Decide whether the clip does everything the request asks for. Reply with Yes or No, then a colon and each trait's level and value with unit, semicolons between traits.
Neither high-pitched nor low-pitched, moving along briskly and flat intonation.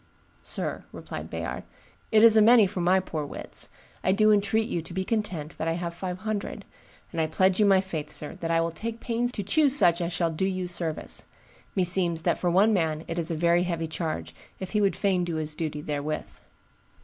No: medium, 180 Hz; fast, 220 wpm; average, 3.5 semitones